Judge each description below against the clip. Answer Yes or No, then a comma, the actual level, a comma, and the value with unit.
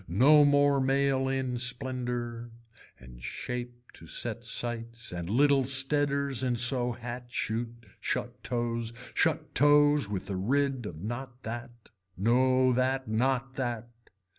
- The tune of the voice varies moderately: No, narrow, 2.3 semitones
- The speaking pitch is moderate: No, low, 125 Hz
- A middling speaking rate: No, slow, 130 wpm